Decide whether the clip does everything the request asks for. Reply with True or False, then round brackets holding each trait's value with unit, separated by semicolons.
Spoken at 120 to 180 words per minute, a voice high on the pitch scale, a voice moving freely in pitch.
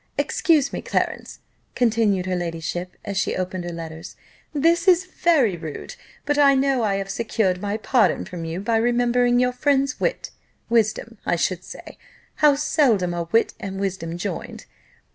True (160 wpm; 215 Hz; 6.7 semitones)